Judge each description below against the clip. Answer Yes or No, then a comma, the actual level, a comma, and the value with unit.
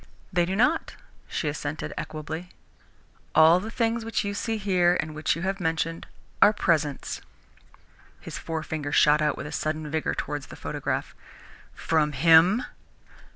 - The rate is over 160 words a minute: No, average, 150 wpm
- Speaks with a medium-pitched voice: Yes, medium, 165 Hz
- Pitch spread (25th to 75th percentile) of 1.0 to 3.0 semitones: No, average, 4.0 semitones